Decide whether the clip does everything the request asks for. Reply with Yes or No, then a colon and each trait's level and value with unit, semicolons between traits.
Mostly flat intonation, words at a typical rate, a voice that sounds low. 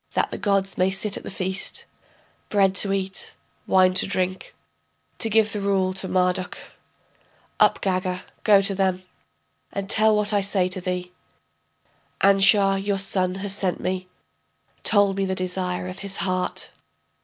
No: narrow, 1.3 semitones; average, 155 wpm; high, 190 Hz